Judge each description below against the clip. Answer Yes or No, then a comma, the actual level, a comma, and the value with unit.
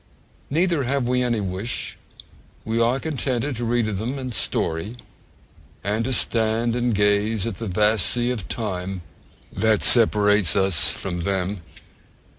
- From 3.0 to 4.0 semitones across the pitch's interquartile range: Yes, average, 3.5 semitones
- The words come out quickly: No, average, 145 wpm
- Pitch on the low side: Yes, low, 110 Hz